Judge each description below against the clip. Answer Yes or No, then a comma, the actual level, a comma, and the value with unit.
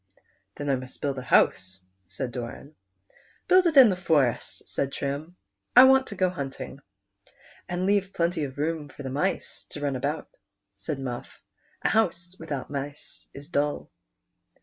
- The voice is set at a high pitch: No, medium, 145 Hz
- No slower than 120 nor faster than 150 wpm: No, average, 170 wpm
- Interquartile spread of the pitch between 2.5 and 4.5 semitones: No, average, 5.2 semitones